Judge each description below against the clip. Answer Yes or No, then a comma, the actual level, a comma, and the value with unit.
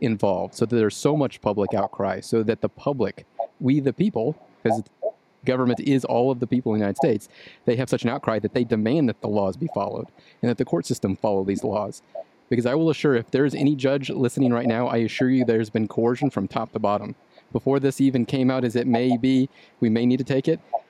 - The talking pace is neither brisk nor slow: No, fast, 240 wpm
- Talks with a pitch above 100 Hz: Yes, low, 125 Hz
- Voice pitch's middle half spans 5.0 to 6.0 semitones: No, average, 3.2 semitones